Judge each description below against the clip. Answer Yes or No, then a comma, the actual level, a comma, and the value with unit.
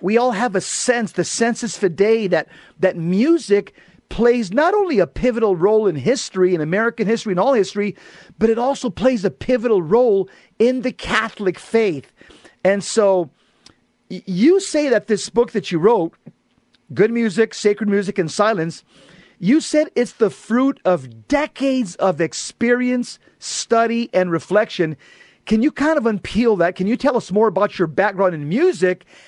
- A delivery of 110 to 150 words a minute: No, average, 165 wpm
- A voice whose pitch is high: Yes, high, 215 Hz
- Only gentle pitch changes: No, average, 4.6 semitones